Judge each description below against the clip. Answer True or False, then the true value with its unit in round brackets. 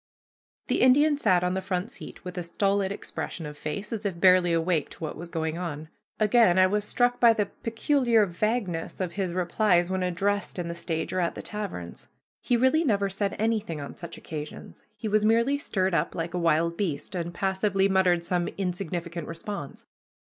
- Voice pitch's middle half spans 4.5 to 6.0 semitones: False (3.6 semitones)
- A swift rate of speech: False (195 wpm)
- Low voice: False (185 Hz)